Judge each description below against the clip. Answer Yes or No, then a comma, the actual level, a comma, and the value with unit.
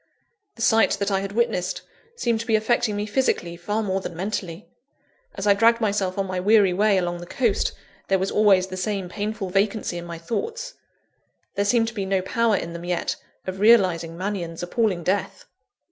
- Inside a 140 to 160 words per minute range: No, average, 190 wpm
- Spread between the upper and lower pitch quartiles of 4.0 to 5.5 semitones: No, average, 3.2 semitones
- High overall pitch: Yes, high, 200 Hz